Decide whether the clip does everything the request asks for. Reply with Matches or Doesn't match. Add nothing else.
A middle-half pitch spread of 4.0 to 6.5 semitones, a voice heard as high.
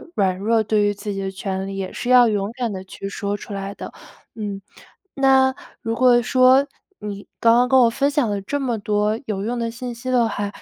Doesn't match